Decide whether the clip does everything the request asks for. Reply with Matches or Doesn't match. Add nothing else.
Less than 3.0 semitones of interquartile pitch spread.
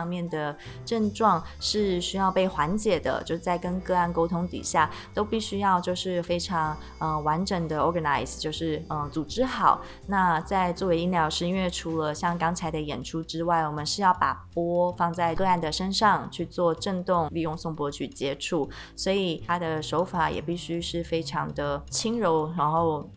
Matches